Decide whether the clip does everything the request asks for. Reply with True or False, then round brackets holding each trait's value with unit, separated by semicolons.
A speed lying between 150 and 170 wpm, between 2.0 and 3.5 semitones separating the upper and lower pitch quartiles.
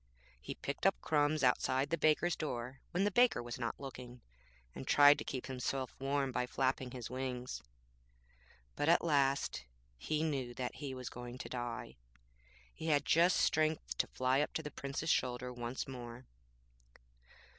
True (165 wpm; 3.0 semitones)